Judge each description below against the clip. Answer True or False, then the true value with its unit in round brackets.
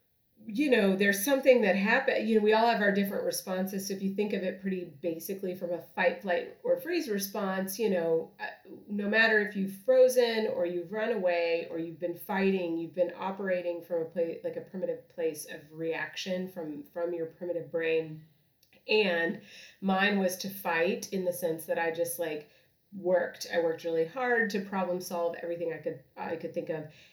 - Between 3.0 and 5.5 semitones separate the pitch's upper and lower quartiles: True (3.8 semitones)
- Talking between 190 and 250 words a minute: True (195 wpm)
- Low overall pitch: False (185 Hz)